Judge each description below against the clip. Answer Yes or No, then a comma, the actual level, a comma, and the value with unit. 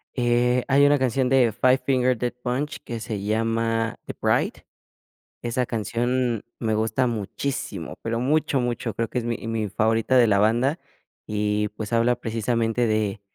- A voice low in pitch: Yes, low, 115 Hz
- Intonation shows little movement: Yes, narrow, 2.3 semitones